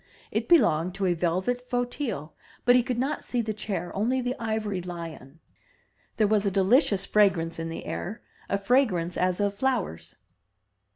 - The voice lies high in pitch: Yes, high, 200 Hz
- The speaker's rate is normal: Yes, average, 175 wpm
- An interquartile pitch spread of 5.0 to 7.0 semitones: Yes, wide, 5.6 semitones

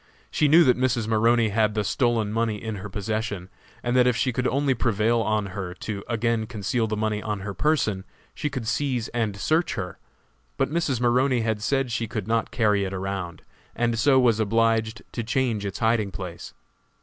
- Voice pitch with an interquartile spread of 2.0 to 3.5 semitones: Yes, average, 2.7 semitones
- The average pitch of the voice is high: No, low, 115 Hz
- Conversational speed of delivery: Yes, average, 195 wpm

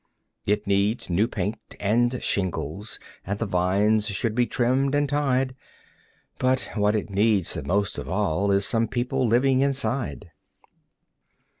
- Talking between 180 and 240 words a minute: No, average, 140 wpm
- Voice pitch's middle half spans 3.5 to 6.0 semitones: Yes, average, 4.2 semitones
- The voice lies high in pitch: No, low, 110 Hz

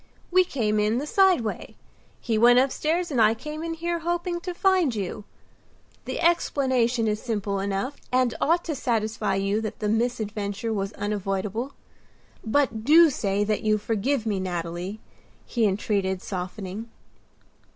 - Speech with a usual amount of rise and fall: No, wide, 5.8 semitones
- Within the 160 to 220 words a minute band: No, average, 150 wpm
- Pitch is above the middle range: Yes, high, 225 Hz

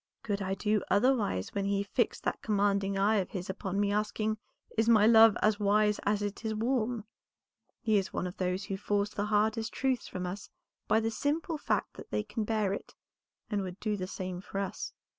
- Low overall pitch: No, high, 205 Hz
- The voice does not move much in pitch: Yes, narrow, 1.9 semitones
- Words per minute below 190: No, fast, 205 wpm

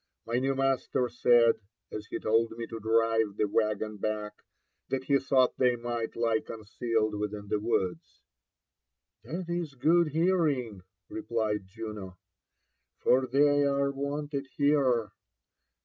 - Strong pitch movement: No, average, 4.3 semitones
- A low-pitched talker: Yes, low, 115 Hz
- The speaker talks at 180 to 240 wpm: No, slow, 135 wpm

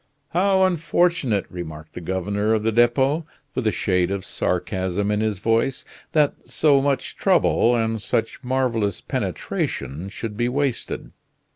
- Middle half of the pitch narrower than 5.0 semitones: No, wide, 5.5 semitones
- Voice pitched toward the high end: No, low, 115 Hz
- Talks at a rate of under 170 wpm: Yes, average, 140 wpm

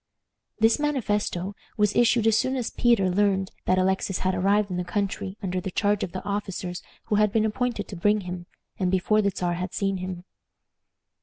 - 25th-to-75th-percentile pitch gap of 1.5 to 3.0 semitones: Yes, narrow, 2.5 semitones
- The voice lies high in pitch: Yes, high, 200 Hz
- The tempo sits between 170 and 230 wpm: Yes, average, 190 wpm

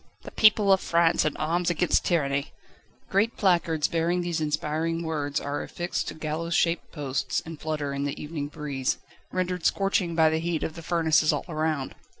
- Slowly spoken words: No, average, 175 wpm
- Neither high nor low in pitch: Yes, medium, 160 Hz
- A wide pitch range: No, narrow, 2.4 semitones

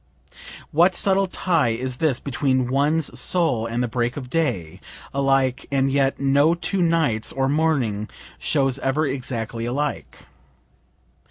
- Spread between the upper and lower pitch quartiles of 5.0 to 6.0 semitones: No, average, 4.0 semitones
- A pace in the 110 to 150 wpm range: Yes, slow, 135 wpm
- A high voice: No, low, 135 Hz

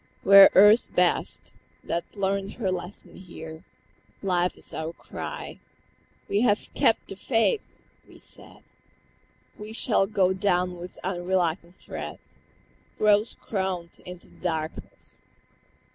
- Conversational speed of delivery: No, slow, 120 wpm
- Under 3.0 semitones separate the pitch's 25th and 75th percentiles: Yes, narrow, 2.6 semitones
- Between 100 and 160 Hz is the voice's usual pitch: No, high, 190 Hz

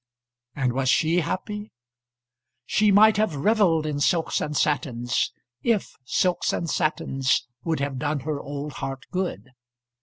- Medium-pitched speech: Yes, medium, 155 Hz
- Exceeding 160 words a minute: No, average, 140 wpm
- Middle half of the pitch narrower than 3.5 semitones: No, average, 5.3 semitones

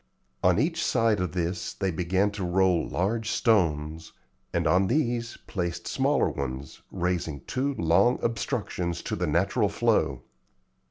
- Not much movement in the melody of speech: No, average, 4.4 semitones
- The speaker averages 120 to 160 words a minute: Yes, average, 140 wpm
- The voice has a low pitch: Yes, very low, 90 Hz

